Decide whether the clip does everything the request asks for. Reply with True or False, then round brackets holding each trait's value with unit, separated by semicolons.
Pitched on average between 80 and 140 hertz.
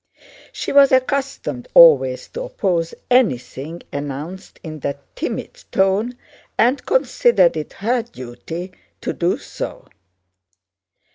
False (185 Hz)